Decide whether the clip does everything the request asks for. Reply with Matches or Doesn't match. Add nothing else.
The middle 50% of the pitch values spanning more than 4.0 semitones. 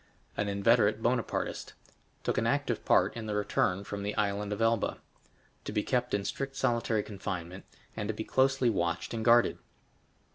Doesn't match